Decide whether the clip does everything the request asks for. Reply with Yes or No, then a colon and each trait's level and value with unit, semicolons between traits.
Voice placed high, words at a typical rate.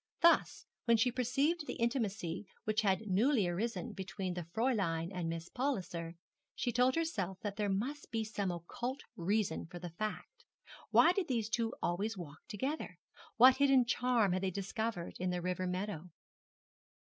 Yes: high, 210 Hz; average, 160 wpm